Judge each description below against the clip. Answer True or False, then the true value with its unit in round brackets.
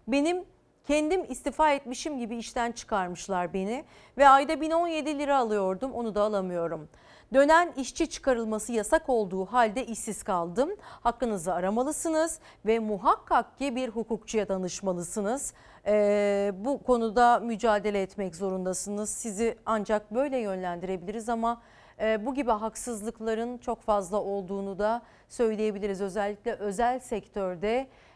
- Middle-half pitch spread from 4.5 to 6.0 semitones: False (4.0 semitones)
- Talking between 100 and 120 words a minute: True (115 wpm)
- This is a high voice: True (225 Hz)